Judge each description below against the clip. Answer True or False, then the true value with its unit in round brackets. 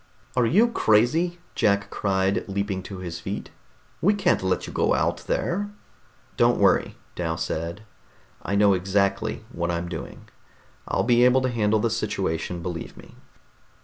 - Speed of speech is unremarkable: True (150 wpm)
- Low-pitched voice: True (100 Hz)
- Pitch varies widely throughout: False (4.7 semitones)